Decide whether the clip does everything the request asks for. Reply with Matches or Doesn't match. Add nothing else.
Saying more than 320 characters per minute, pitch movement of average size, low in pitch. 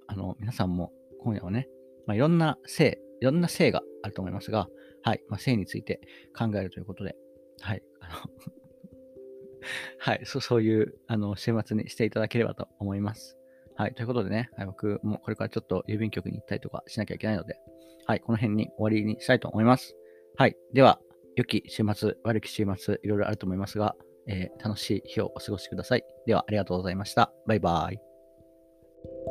Matches